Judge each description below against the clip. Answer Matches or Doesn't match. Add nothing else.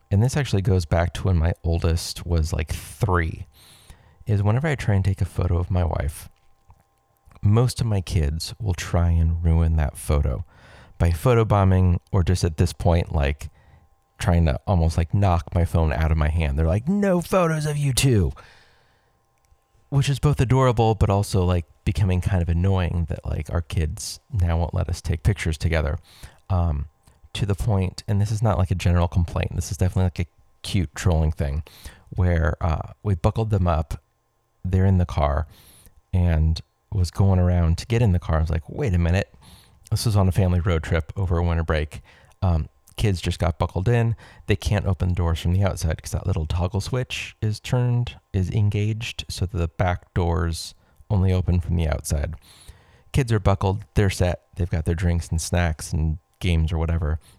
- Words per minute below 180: Doesn't match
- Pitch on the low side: Matches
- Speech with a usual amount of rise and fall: Matches